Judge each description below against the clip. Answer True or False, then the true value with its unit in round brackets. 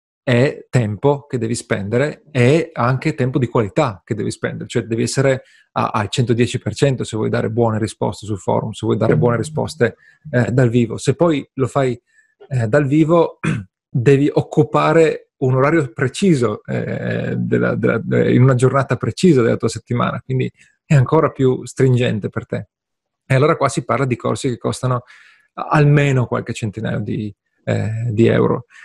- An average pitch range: True (4.0 semitones)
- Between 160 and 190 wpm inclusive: True (165 wpm)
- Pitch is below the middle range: True (125 Hz)